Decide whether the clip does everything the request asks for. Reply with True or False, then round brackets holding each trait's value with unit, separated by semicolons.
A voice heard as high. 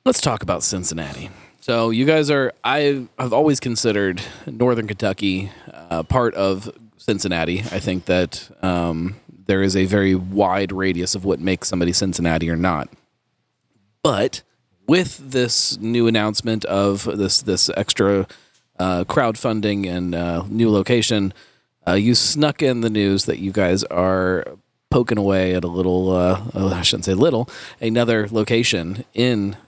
False (100 Hz)